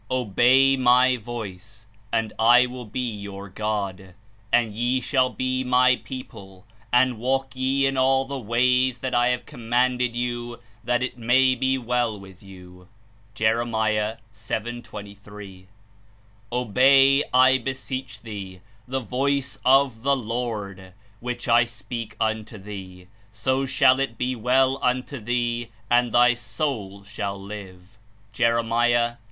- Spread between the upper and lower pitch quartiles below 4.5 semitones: Yes, average, 3.1 semitones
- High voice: No, low, 120 Hz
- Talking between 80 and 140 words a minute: Yes, slow, 135 wpm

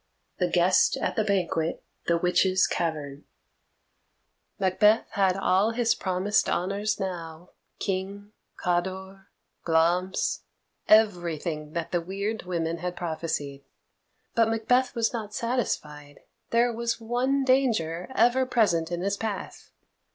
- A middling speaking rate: No, slow, 105 wpm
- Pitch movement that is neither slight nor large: Yes, average, 4.5 semitones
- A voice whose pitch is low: No, high, 190 Hz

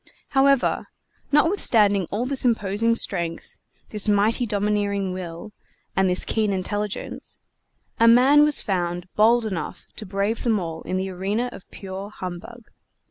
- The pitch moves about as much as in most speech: Yes, average, 3.5 semitones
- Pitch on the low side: No, high, 205 Hz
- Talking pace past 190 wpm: No, slow, 135 wpm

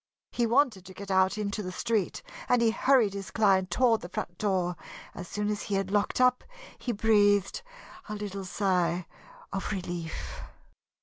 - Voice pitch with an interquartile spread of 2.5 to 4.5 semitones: Yes, average, 2.8 semitones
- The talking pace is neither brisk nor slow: Yes, average, 170 wpm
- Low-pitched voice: No, high, 200 Hz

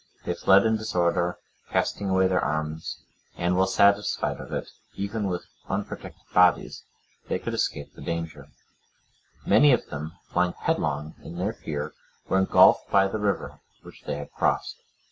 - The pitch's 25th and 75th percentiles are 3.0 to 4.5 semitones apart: Yes, average, 3.7 semitones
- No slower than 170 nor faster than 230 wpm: No, average, 150 wpm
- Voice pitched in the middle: No, very low, 90 Hz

